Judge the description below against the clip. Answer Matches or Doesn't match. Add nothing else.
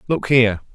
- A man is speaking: Matches